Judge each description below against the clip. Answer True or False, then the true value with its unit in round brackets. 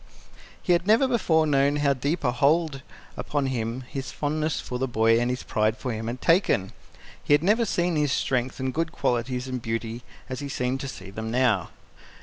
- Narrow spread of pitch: False (4.2 semitones)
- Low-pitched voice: True (130 Hz)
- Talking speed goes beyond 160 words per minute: True (200 wpm)